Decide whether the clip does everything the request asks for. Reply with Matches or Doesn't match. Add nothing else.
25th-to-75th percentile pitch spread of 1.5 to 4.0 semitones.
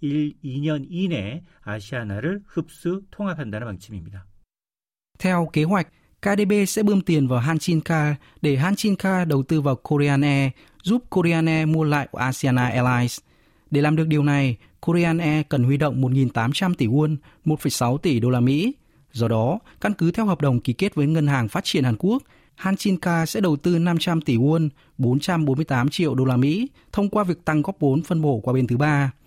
Doesn't match